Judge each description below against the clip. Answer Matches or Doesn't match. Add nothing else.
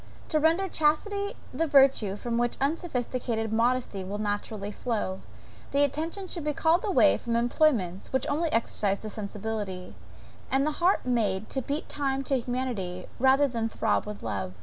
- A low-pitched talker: Doesn't match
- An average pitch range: Doesn't match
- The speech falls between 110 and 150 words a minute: Doesn't match